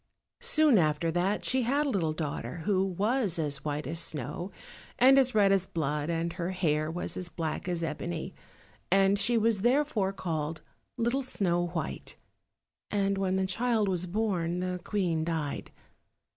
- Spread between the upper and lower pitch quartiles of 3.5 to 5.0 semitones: Yes, average, 4.3 semitones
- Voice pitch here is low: No, medium, 180 Hz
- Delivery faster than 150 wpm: Yes, average, 160 wpm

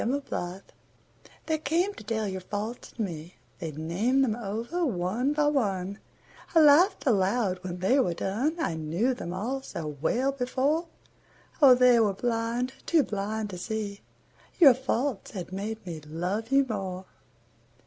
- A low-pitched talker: No, high, 220 Hz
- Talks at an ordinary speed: Yes, average, 155 wpm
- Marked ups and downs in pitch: Yes, wide, 6.0 semitones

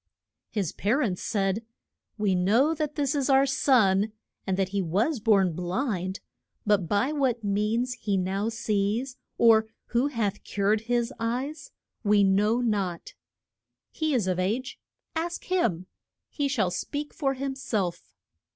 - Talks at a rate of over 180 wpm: No, average, 145 wpm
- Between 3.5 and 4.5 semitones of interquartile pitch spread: No, wide, 5.4 semitones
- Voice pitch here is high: Yes, high, 220 Hz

